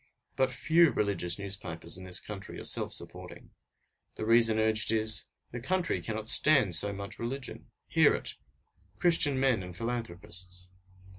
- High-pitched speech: No, low, 110 Hz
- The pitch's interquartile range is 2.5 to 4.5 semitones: No, average, 4.9 semitones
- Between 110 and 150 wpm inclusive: Yes, average, 145 wpm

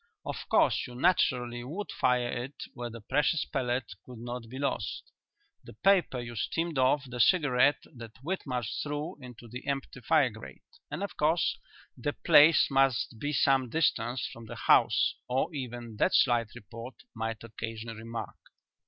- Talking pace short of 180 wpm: Yes, average, 160 wpm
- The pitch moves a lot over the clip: No, average, 3.7 semitones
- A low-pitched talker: Yes, low, 125 Hz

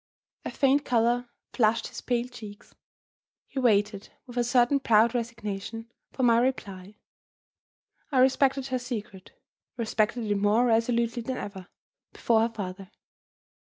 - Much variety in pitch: No, average, 2.8 semitones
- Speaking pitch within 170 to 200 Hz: No, high, 230 Hz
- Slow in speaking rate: Yes, slow, 130 wpm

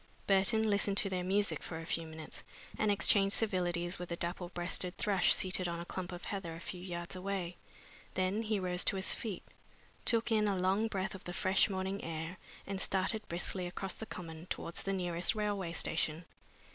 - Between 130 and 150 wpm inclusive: No, average, 195 wpm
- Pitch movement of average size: No, narrow, 2.2 semitones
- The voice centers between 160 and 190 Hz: Yes, medium, 185 Hz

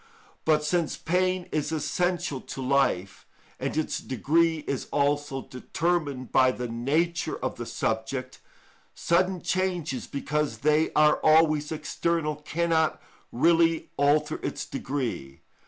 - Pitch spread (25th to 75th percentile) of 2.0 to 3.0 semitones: No, average, 3.7 semitones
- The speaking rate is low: Yes, slow, 120 wpm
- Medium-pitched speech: Yes, medium, 150 Hz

